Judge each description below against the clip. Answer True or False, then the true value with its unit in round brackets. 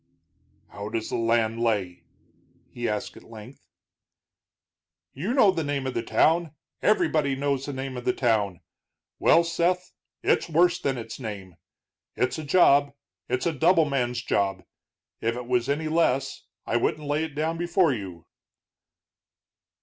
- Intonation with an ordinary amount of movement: False (5.7 semitones)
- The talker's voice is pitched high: False (135 Hz)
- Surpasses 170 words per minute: False (150 wpm)